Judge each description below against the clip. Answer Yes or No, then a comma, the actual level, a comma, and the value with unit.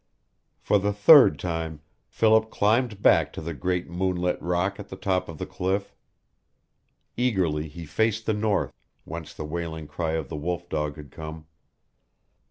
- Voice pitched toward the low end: Yes, very low, 90 Hz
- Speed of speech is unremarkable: Yes, average, 160 wpm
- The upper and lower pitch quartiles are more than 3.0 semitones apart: Yes, average, 4.4 semitones